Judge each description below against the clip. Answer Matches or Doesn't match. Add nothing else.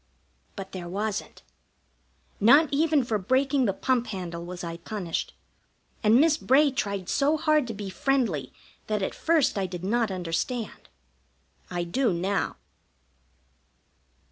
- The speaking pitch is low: Doesn't match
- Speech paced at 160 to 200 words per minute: Doesn't match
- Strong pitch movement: Matches